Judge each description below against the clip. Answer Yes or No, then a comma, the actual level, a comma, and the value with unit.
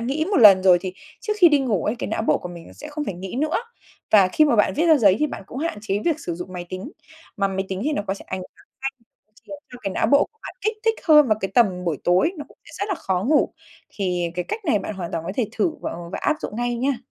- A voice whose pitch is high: Yes, high, 215 Hz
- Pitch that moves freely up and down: Yes, wide, 8.2 semitones